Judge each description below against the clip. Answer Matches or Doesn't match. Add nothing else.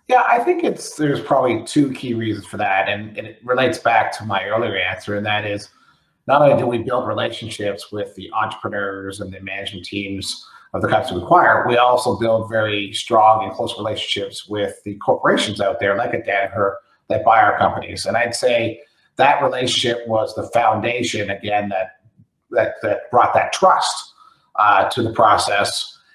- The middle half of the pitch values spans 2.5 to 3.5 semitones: Matches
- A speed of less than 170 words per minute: Doesn't match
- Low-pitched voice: Matches